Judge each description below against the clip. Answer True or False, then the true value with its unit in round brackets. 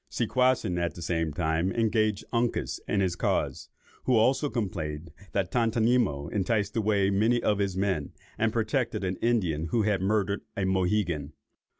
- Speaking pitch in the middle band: False (100 Hz)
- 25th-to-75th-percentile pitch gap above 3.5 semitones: True (4.3 semitones)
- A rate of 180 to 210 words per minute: False (155 wpm)